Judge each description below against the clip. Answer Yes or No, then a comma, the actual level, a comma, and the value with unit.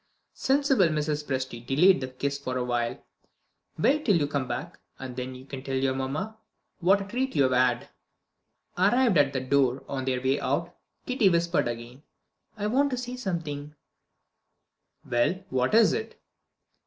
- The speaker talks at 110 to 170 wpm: Yes, average, 165 wpm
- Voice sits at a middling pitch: Yes, medium, 145 Hz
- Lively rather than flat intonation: Yes, wide, 7.0 semitones